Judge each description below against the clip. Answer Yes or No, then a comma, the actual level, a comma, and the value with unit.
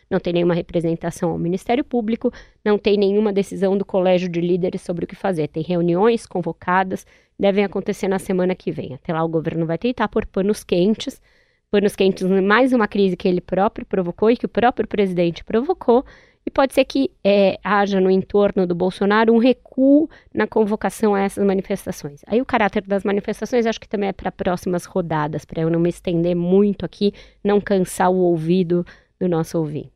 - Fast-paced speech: Yes, fast, 190 wpm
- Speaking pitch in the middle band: No, high, 195 Hz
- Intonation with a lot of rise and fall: No, average, 3.2 semitones